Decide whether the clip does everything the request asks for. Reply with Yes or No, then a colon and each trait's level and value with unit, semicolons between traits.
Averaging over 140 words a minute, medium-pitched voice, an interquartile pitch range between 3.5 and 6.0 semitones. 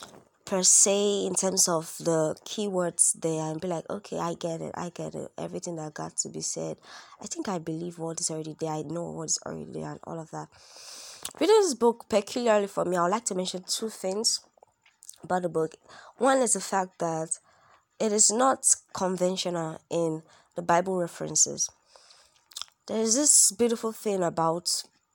Yes: average, 180 wpm; medium, 180 Hz; average, 4.2 semitones